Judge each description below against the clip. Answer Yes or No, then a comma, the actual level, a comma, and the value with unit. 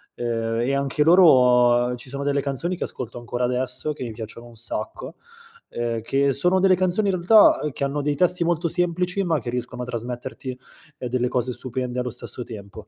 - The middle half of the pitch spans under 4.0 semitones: No, average, 5.0 semitones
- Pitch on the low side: Yes, low, 130 Hz